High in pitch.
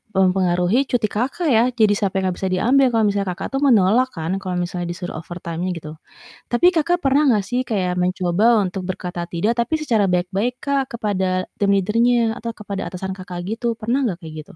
Yes: high, 200 Hz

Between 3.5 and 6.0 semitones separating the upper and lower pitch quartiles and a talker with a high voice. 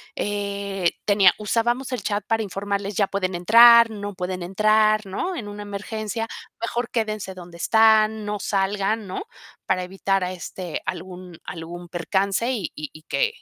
No: average, 2.8 semitones; high, 200 Hz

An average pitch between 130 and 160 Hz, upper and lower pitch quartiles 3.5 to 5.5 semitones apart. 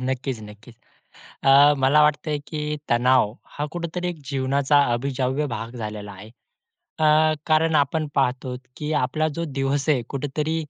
No: medium, 140 Hz; average, 3.1 semitones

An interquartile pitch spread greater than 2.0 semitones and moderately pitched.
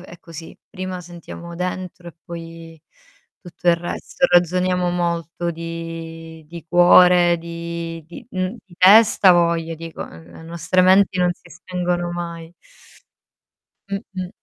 No: narrow, 1.4 semitones; medium, 175 Hz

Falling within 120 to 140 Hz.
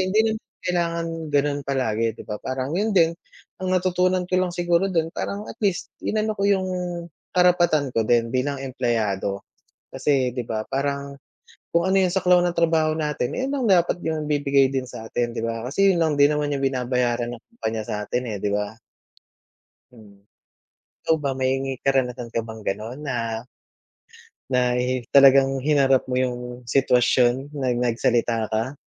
Yes: low, 135 Hz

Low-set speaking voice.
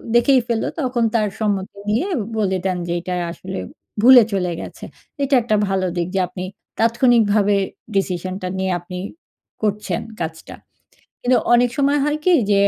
No: high, 205 Hz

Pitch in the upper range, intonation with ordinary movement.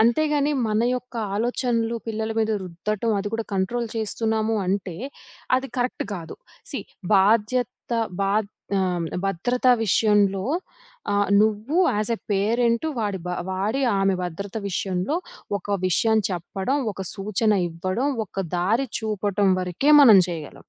Yes: high, 210 Hz; average, 3.3 semitones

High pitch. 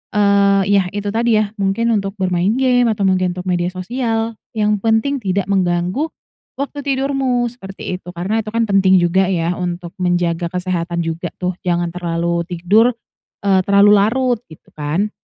Yes: high, 195 Hz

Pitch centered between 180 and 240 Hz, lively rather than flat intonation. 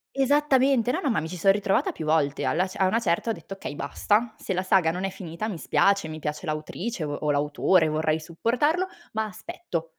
Yes: medium, 185 Hz; wide, 6.2 semitones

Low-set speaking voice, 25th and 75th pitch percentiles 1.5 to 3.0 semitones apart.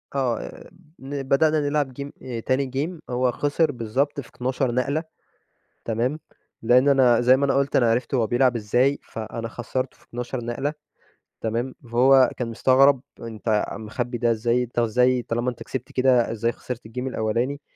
Yes: low, 125 Hz; narrow, 2.5 semitones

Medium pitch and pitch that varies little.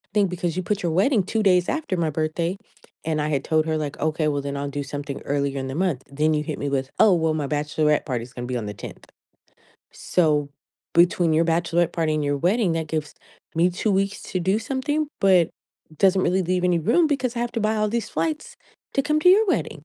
No: medium, 170 Hz; average, 4.8 semitones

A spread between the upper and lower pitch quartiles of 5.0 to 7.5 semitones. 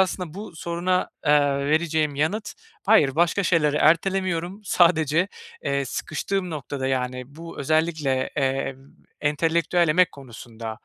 No: average, 3.8 semitones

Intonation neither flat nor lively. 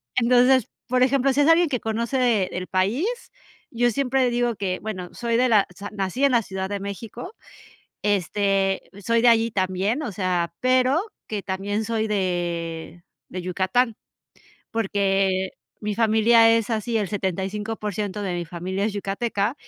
Yes: average, 3.9 semitones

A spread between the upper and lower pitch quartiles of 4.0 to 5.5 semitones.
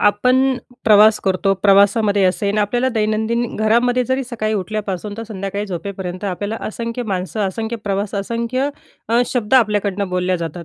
No: average, 2.8 semitones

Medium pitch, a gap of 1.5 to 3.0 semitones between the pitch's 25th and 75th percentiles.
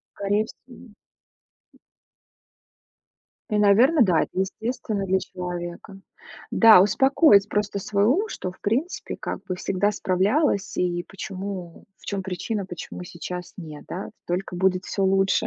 No: high, 195 Hz; narrow, 2.6 semitones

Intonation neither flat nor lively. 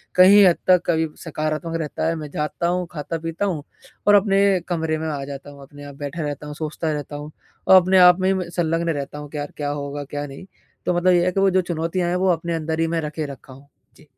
Yes: average, 3.3 semitones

